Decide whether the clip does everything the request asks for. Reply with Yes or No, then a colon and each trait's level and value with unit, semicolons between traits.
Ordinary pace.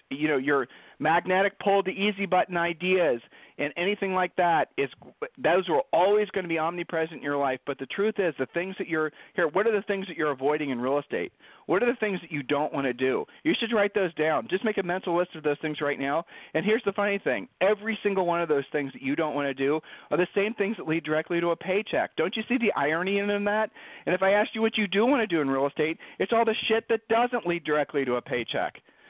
No: fast, 260 wpm